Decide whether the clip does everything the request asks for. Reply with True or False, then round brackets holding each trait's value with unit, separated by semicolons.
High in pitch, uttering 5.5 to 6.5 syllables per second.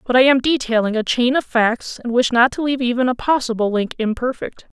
True (245 Hz; 5.8 syllables/s)